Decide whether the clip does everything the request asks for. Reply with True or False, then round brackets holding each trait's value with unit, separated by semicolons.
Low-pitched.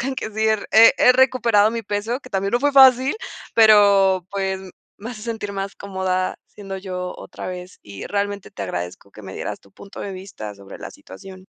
False (200 Hz)